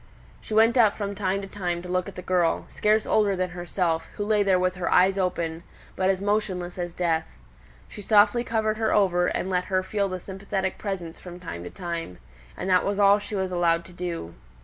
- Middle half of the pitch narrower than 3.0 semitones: Yes, narrow, 2.4 semitones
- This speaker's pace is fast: Yes, fast, 215 wpm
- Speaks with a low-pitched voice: No, medium, 185 Hz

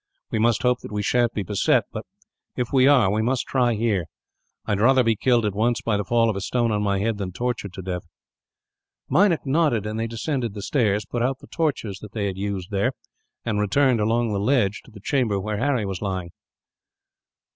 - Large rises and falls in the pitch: No, average, 3.4 semitones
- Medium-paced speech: No, fast, 220 wpm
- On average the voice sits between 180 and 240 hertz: No, low, 110 Hz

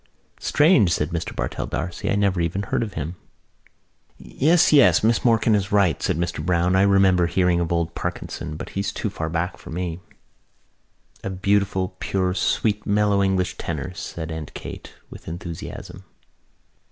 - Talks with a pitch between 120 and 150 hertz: No, very low, 90 Hz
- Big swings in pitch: No, average, 3.0 semitones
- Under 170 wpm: Yes, average, 160 wpm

